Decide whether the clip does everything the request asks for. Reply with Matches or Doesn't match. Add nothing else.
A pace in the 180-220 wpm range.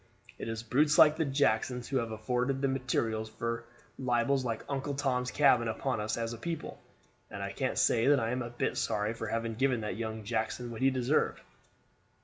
Matches